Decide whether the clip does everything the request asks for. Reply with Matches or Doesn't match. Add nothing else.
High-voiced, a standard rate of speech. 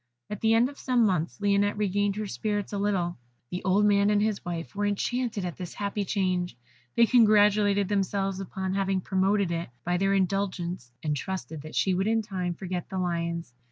Matches